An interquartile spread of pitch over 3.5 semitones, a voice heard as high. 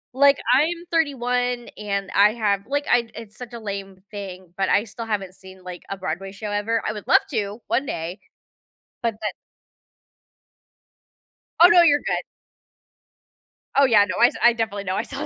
Yes: average, 4.0 semitones; high, 215 Hz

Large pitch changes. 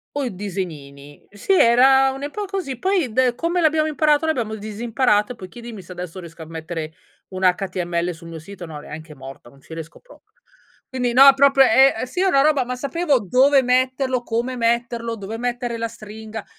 Yes: wide, 6.6 semitones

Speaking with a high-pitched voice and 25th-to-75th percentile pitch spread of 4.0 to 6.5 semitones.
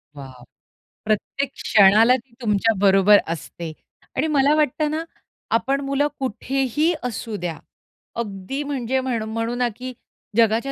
Yes: high, 235 Hz; average, 4.7 semitones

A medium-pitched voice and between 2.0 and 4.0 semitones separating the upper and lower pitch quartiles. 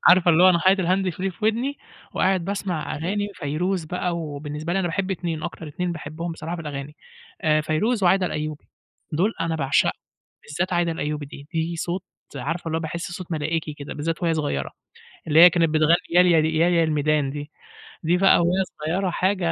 Yes: medium, 165 Hz; average, 2.8 semitones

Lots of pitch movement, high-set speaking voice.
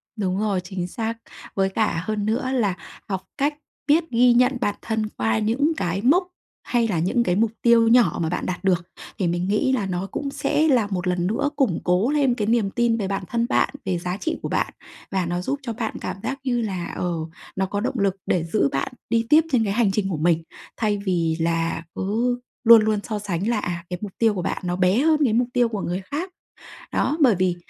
No: average, 4.8 semitones; high, 210 Hz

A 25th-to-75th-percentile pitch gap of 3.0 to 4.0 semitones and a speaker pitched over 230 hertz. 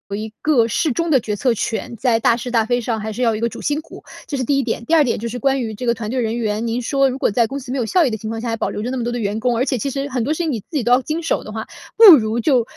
Yes: average, 3.3 semitones; high, 240 Hz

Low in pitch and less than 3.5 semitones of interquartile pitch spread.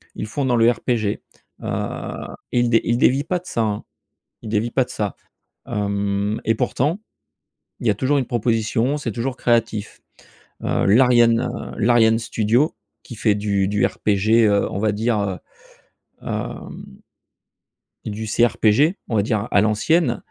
Yes: low, 115 Hz; average, 2.7 semitones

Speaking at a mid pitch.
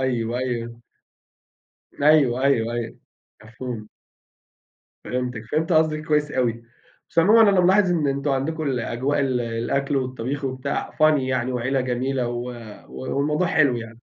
No: low, 130 Hz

